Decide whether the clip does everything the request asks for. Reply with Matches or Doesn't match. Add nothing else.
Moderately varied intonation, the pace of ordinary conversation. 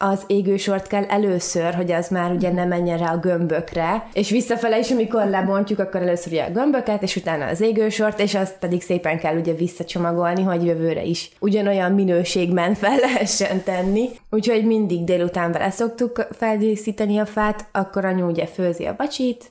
Doesn't match